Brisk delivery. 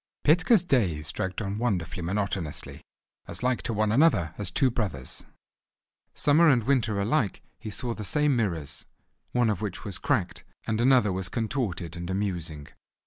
No: average, 155 wpm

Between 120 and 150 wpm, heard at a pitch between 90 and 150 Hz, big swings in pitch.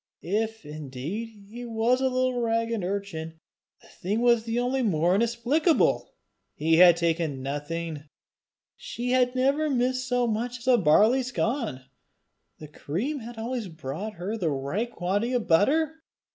No: average, 145 wpm; high, 225 Hz; wide, 6.8 semitones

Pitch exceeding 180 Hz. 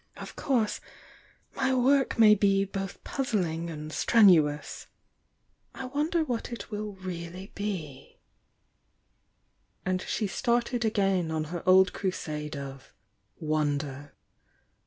Yes: high, 190 Hz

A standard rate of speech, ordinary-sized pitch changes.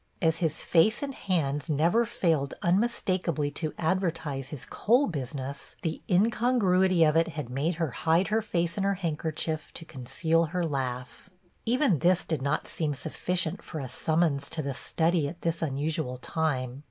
Yes: average, 165 wpm; average, 4.0 semitones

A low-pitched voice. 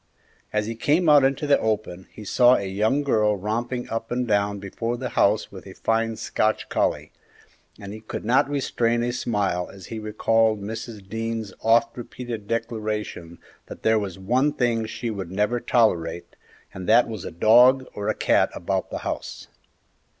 Yes: low, 110 Hz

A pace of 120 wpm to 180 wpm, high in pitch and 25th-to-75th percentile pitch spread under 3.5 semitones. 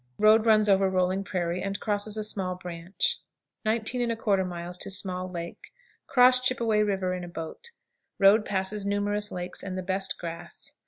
Yes: average, 155 wpm; high, 195 Hz; average, 2.7 semitones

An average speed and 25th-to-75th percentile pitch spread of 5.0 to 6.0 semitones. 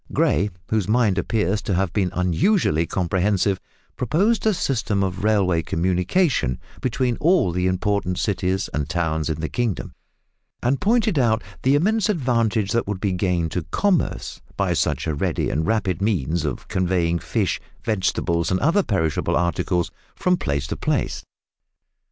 Yes: average, 150 wpm; wide, 5.6 semitones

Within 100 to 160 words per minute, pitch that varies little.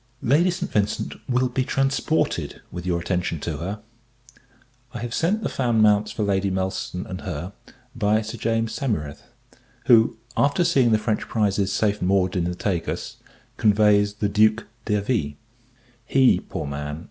No: average, 155 wpm; average, 4.2 semitones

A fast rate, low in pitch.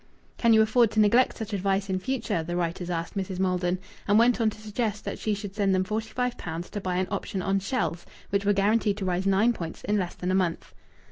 No: fast, 245 wpm; high, 200 Hz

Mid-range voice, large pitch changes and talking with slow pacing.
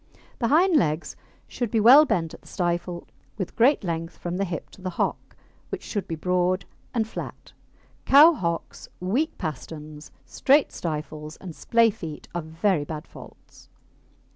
No: medium, 180 Hz; wide, 5.9 semitones; average, 160 wpm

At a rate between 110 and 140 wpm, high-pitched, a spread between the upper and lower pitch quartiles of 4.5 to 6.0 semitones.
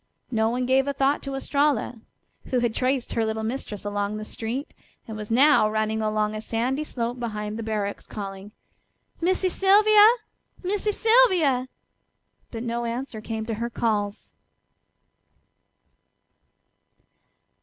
No: slow, 135 wpm; high, 235 Hz; average, 4.1 semitones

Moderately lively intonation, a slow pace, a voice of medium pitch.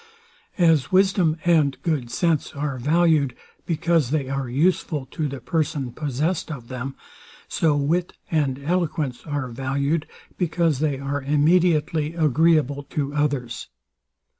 Yes: average, 3.1 semitones; slow, 125 wpm; medium, 150 Hz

